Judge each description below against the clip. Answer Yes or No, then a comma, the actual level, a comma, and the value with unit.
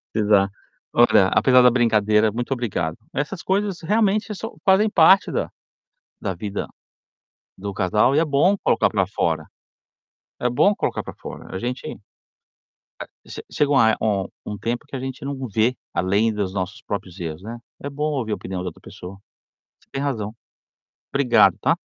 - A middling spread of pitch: No, wide, 6.0 semitones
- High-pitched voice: No, low, 115 Hz